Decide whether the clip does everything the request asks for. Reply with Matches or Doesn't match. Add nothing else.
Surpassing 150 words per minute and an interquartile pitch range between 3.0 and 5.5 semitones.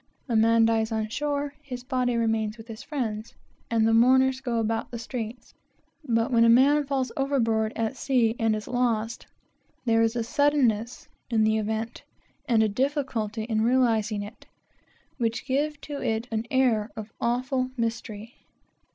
Doesn't match